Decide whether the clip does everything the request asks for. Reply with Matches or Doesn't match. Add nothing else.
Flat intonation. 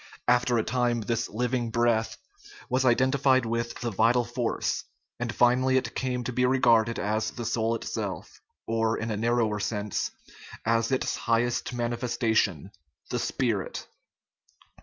Matches